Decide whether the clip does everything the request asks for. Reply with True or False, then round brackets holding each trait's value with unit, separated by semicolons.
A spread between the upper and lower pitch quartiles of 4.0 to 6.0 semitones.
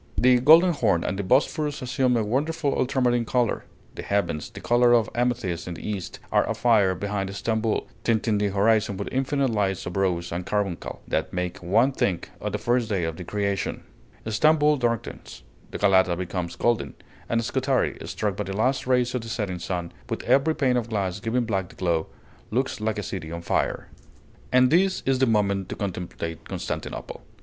True (4.7 semitones)